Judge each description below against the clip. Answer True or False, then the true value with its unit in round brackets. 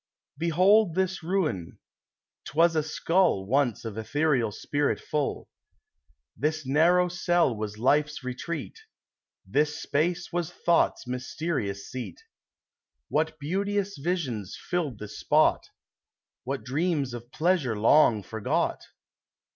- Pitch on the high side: False (150 Hz)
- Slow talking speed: True (115 wpm)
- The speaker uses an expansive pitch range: True (5.8 semitones)